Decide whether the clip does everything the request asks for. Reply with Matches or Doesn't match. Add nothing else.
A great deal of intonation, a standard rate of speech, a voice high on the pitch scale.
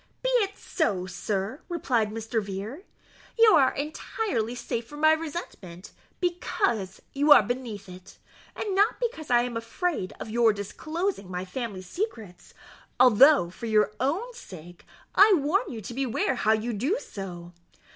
Matches